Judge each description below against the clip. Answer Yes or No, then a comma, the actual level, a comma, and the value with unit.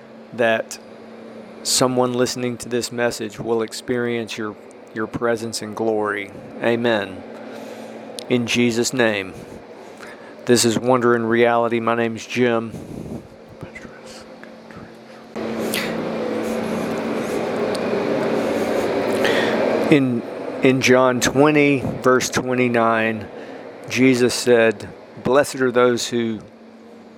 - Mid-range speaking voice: No, low, 120 Hz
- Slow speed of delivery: Yes, slow, 85 wpm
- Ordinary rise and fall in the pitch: No, narrow, 1.8 semitones